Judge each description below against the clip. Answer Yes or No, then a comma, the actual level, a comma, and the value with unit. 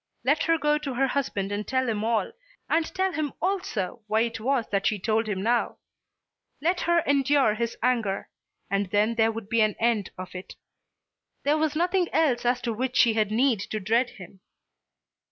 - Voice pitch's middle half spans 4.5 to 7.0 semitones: Yes, average, 4.9 semitones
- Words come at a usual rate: Yes, average, 190 wpm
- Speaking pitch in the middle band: No, high, 235 Hz